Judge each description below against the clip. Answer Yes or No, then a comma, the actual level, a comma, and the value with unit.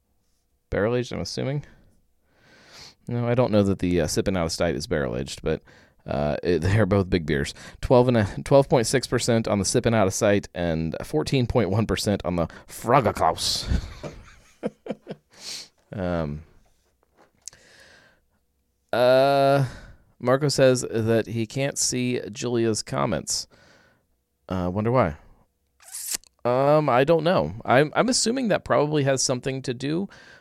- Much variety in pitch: Yes, wide, 6.6 semitones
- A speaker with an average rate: No, slow, 130 wpm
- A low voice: Yes, low, 115 Hz